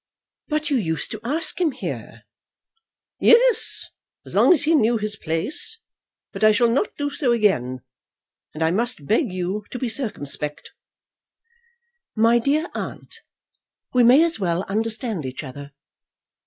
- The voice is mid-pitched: No, high, 230 Hz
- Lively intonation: Yes, wide, 7.9 semitones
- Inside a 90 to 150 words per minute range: Yes, average, 145 wpm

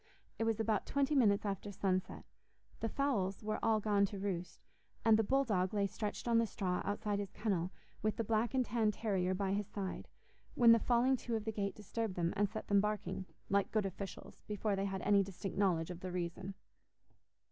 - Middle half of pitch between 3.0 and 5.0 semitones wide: No, narrow, 2.6 semitones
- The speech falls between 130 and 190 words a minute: No, fast, 205 wpm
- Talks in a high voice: Yes, high, 205 Hz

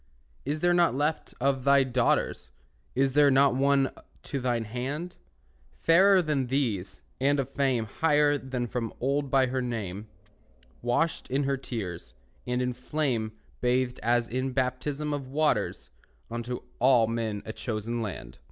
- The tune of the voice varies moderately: Yes, average, 3.0 semitones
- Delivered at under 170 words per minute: Yes, average, 150 wpm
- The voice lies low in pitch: Yes, low, 130 Hz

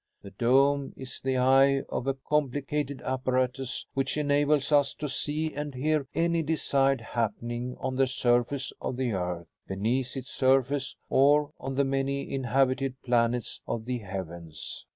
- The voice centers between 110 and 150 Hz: Yes, low, 135 Hz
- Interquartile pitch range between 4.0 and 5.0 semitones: No, narrow, 2.4 semitones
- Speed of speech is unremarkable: Yes, average, 150 wpm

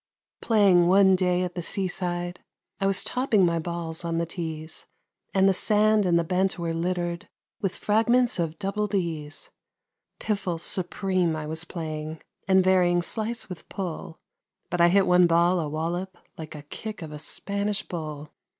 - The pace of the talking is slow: No, average, 165 wpm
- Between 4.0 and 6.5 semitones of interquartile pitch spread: No, average, 2.7 semitones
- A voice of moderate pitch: Yes, medium, 175 Hz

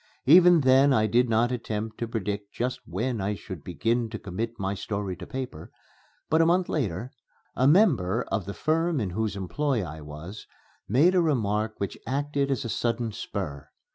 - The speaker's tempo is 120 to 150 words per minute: No, average, 180 wpm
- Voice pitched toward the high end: No, low, 115 Hz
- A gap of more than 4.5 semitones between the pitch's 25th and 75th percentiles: Yes, average, 5.2 semitones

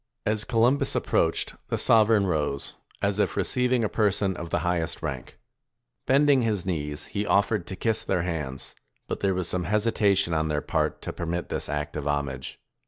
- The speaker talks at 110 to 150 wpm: No, average, 180 wpm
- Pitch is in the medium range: No, very low, 95 Hz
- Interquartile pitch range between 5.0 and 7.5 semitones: Yes, average, 5.3 semitones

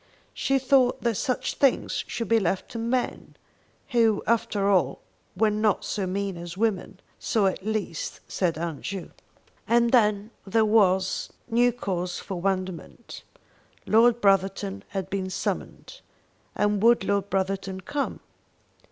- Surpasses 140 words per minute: No, slow, 135 wpm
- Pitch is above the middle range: Yes, high, 200 Hz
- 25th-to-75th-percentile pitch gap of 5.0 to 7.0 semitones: No, average, 3.3 semitones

